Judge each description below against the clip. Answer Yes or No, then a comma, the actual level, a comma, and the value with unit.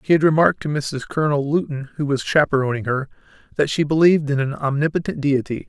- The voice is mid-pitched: Yes, medium, 145 Hz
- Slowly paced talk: No, average, 190 wpm